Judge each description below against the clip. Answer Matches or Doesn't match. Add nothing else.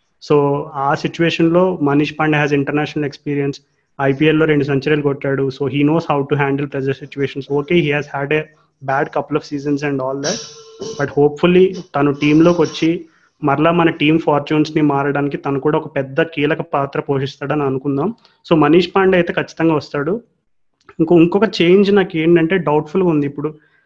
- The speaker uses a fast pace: Matches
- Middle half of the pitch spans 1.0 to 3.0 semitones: Matches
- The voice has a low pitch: Doesn't match